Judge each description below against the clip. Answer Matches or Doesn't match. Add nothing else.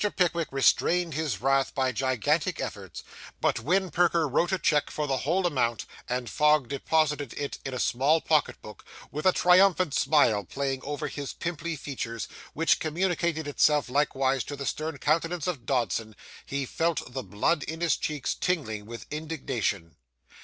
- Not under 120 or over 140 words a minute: Doesn't match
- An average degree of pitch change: Matches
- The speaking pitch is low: Doesn't match